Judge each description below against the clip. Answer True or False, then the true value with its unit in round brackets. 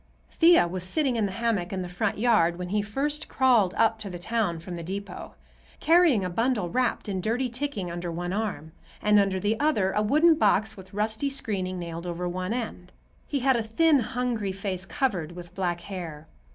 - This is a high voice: True (205 Hz)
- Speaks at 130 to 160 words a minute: False (200 wpm)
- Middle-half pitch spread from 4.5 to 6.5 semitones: True (5.0 semitones)